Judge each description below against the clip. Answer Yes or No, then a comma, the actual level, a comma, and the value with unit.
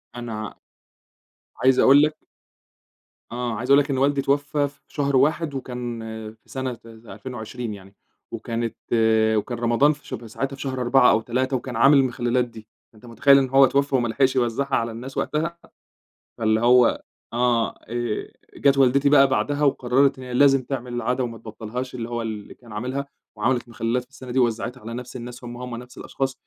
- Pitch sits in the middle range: No, low, 125 Hz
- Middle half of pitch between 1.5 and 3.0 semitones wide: Yes, narrow, 2.6 semitones